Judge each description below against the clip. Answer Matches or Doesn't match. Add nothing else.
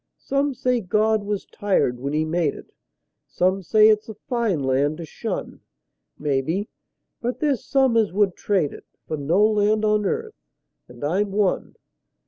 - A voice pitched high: Matches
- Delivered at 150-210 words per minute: Matches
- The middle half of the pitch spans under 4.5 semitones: Doesn't match